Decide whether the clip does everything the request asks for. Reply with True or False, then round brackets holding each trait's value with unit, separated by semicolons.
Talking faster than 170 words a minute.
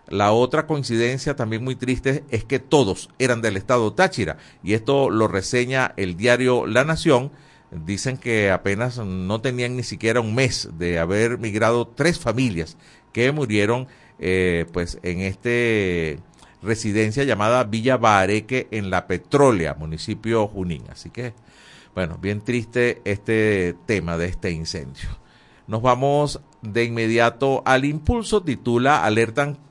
False (135 wpm)